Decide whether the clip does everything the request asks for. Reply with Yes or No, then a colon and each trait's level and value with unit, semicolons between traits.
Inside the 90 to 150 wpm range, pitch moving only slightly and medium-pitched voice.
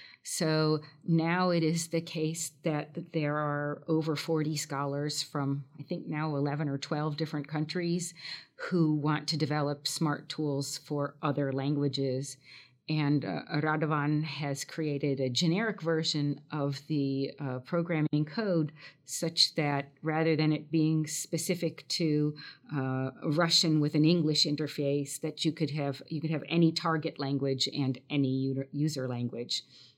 Yes: average, 140 wpm; narrow, 2.1 semitones; medium, 150 Hz